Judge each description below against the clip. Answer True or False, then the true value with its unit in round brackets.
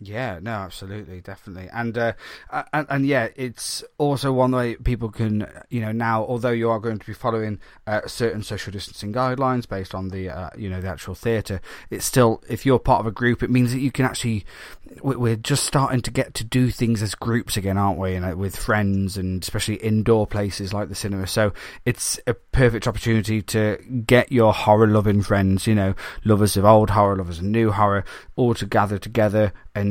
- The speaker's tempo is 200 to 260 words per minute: True (205 wpm)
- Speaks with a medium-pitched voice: False (110 Hz)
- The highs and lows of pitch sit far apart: False (3.1 semitones)